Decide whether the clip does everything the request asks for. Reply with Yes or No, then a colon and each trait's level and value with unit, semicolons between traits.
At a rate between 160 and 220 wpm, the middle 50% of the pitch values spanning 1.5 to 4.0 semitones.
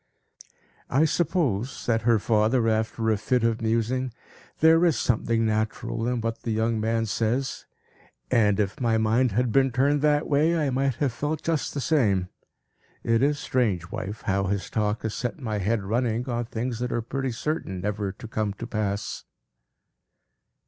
Yes: average, 170 wpm; average, 3.2 semitones